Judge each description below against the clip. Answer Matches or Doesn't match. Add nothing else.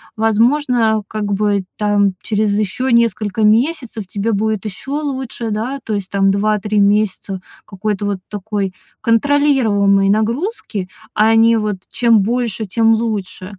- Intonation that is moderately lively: Doesn't match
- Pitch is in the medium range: Doesn't match